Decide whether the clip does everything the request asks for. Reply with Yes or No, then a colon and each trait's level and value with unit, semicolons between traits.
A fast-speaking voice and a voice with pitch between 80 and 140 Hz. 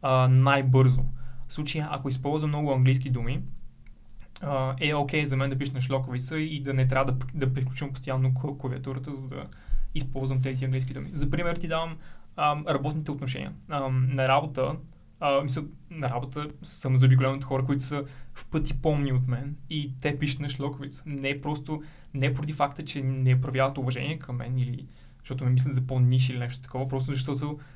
Yes: fast, 185 wpm; low, 135 Hz